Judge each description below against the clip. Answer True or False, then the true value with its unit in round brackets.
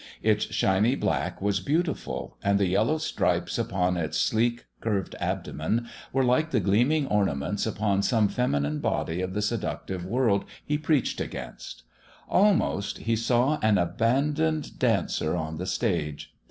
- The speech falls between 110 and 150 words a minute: True (140 wpm)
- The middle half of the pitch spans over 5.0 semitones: True (5.4 semitones)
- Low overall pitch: True (105 Hz)